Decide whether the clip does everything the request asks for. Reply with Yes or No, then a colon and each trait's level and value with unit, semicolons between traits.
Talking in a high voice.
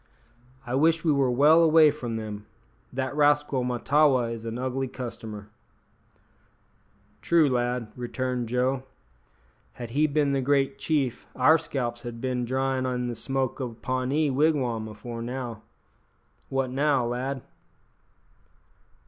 No: low, 130 Hz